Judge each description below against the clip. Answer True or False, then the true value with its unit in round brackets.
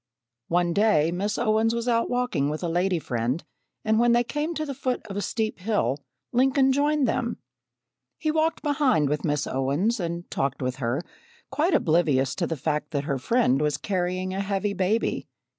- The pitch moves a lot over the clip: True (8.1 semitones)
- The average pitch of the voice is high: True (195 Hz)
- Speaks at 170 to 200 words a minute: True (185 wpm)